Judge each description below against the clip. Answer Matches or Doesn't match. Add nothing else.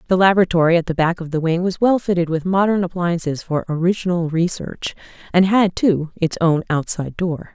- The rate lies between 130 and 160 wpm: Doesn't match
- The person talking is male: Doesn't match